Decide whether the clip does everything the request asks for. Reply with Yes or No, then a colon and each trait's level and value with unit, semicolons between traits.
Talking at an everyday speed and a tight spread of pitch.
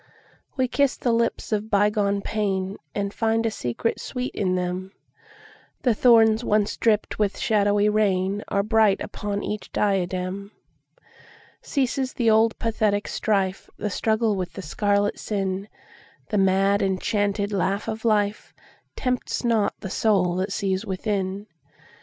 No: slow, 115 wpm; narrow, 2.2 semitones